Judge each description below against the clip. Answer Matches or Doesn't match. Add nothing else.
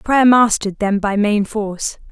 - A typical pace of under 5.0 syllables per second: Matches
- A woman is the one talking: Matches